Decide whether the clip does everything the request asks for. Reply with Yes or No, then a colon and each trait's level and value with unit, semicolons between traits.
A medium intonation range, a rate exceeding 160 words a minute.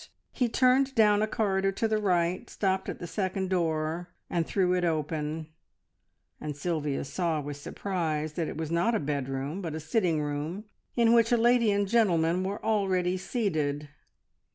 Yes: average, 4.9 semitones; average, 175 wpm